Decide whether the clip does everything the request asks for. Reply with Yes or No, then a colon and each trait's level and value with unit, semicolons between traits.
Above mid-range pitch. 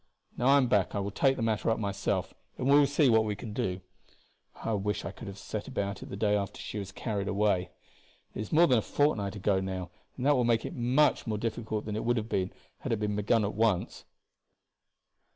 No: low, 105 Hz